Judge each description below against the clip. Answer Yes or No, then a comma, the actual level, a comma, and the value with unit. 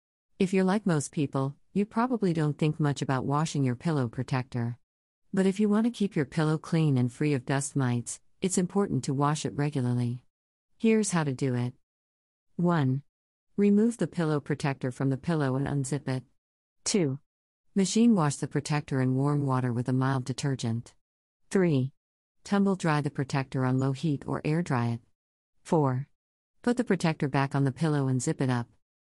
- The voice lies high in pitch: No, medium, 140 Hz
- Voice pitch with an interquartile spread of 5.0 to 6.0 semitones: No, average, 4.4 semitones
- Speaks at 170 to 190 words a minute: Yes, average, 180 wpm